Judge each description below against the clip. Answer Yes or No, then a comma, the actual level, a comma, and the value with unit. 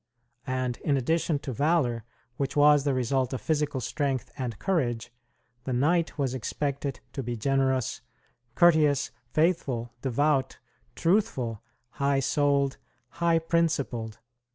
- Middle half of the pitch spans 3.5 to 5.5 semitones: No, average, 3.1 semitones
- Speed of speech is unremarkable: No, slow, 120 wpm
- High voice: No, medium, 140 Hz